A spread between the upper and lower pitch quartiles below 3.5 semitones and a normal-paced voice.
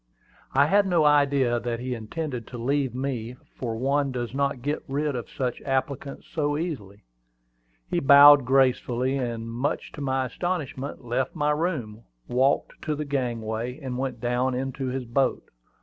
Yes: average, 2.8 semitones; average, 160 wpm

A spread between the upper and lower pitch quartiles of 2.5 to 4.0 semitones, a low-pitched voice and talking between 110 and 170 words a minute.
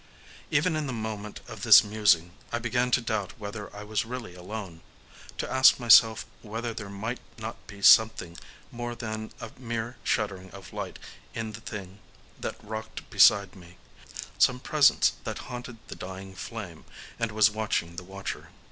Yes: average, 2.9 semitones; low, 110 Hz; average, 160 wpm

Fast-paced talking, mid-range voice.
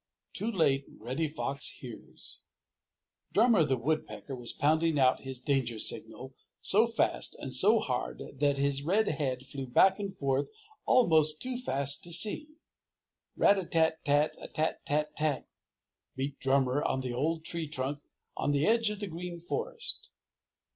No: average, 155 wpm; medium, 150 Hz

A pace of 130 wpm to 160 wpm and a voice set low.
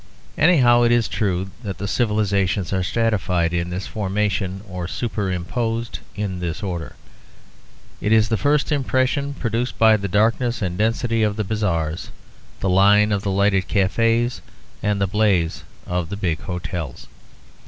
Yes: average, 150 wpm; low, 105 Hz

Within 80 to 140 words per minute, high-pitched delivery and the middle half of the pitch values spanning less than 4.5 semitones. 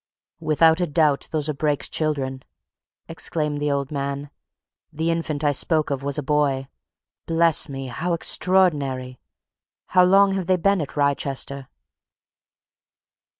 No: slow, 135 wpm; medium, 150 Hz; average, 3.1 semitones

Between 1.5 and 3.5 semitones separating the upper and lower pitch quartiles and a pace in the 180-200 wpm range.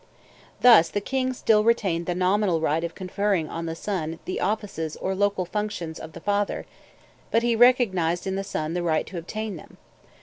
No: average, 4.1 semitones; average, 190 wpm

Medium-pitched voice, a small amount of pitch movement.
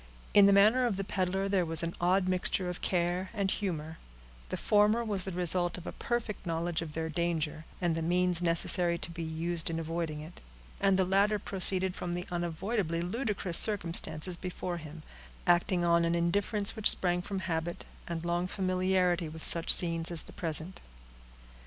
Yes: medium, 175 Hz; narrow, 2.3 semitones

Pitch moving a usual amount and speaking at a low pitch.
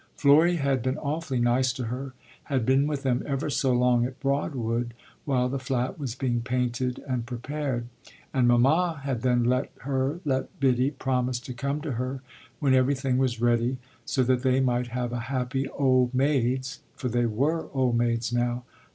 No: narrow, 2.1 semitones; low, 130 Hz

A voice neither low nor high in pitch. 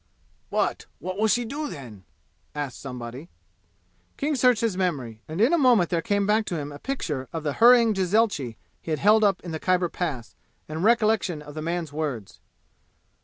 Yes: medium, 175 Hz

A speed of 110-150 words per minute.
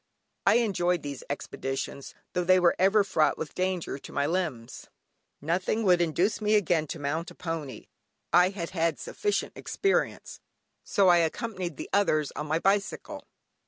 No: average, 160 wpm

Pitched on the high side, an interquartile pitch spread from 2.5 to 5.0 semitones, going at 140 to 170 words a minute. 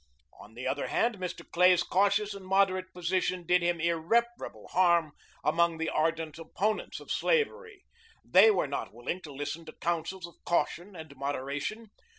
No: medium, 175 Hz; average, 3.6 semitones; average, 160 wpm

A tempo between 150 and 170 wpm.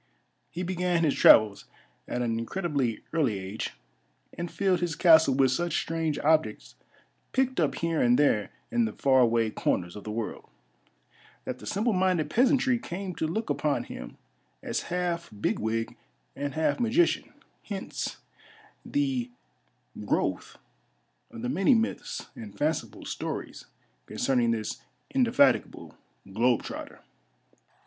No: average, 140 wpm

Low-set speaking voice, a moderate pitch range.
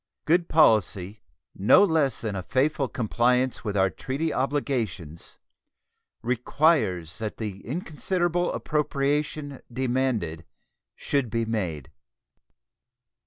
No: low, 125 Hz; wide, 6.1 semitones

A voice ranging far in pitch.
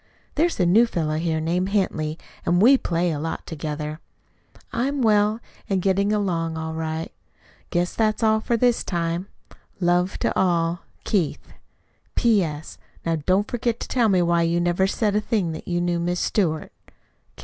No: average, 4.1 semitones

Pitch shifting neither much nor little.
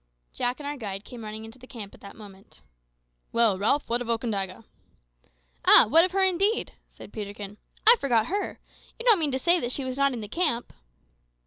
No: wide, 5.7 semitones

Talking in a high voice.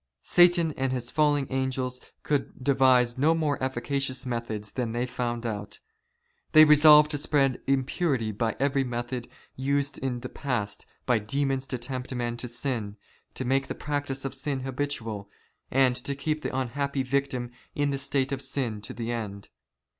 No: low, 130 Hz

